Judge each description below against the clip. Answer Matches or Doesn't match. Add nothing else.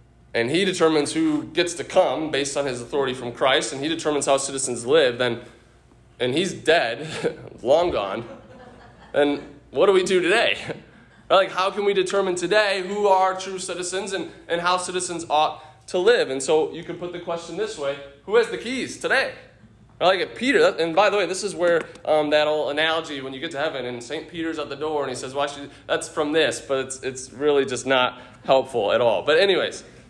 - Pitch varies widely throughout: Doesn't match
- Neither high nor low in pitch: Matches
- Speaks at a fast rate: Matches